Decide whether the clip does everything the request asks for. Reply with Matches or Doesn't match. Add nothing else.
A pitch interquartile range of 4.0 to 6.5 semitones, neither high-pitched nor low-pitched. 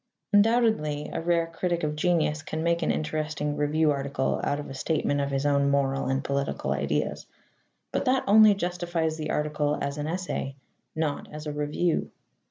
Doesn't match